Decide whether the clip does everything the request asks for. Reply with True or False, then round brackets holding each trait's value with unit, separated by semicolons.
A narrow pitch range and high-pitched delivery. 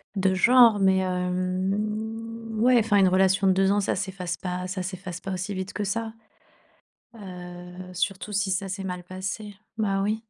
True (2.2 semitones; 195 Hz)